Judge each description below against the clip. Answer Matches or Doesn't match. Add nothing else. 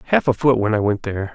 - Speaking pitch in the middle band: Doesn't match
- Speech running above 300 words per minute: Matches